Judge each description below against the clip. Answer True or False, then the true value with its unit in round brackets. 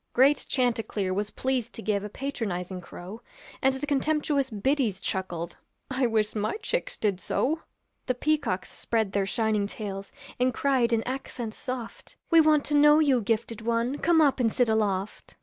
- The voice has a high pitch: True (235 Hz)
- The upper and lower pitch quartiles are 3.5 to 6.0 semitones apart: True (4.7 semitones)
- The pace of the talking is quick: False (165 wpm)